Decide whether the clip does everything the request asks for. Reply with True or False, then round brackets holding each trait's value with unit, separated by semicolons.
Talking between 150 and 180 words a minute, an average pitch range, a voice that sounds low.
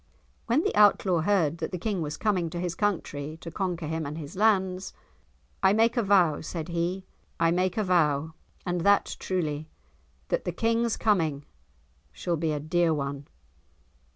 False (170 wpm; 3.8 semitones; 175 Hz)